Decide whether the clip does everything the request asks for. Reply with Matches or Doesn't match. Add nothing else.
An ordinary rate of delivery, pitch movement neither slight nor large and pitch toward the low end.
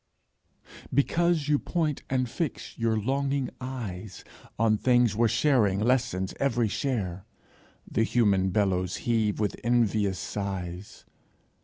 Doesn't match